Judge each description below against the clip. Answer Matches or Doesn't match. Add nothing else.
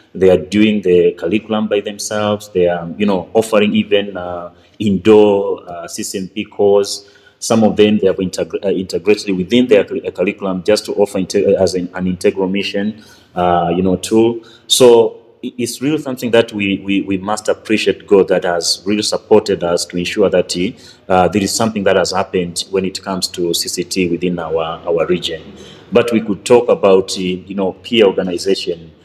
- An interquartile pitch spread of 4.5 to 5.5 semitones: Doesn't match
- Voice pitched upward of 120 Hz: Doesn't match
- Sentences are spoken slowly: Doesn't match